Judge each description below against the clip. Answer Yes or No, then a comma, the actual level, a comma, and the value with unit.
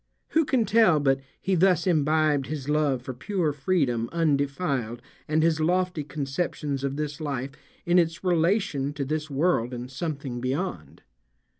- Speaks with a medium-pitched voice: Yes, medium, 150 Hz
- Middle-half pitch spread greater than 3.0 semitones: Yes, average, 4.1 semitones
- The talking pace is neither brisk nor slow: Yes, average, 150 wpm